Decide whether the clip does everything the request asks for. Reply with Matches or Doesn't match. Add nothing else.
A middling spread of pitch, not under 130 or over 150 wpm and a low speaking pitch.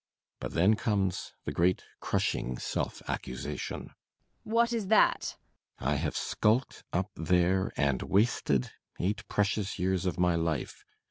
Matches